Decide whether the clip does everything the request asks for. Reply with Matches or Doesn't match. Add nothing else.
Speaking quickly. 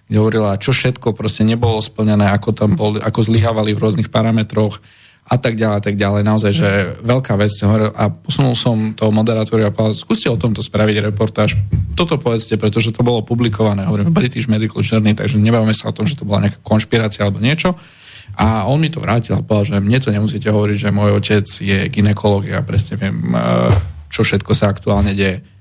Matches